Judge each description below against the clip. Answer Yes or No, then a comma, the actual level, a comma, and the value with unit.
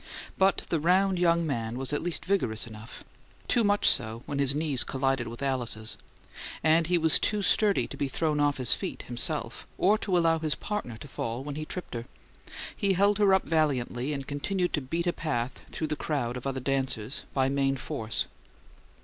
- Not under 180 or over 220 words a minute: Yes, average, 195 wpm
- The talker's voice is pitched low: No, medium, 145 Hz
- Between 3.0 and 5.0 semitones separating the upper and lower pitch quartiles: No, wide, 5.4 semitones